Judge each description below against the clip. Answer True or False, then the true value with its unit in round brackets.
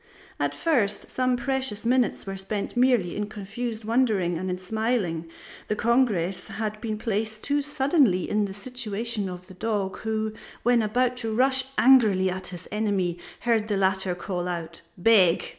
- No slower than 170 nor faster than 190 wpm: False (160 wpm)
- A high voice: True (215 Hz)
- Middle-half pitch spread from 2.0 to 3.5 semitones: False (4.2 semitones)